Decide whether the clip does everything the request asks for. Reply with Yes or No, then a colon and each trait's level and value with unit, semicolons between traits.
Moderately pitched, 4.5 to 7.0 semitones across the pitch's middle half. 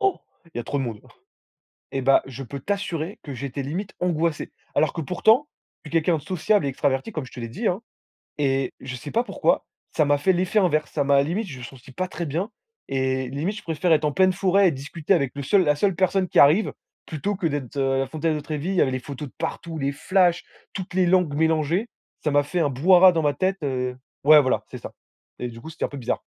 Yes: medium, 155 Hz; average, 5.0 semitones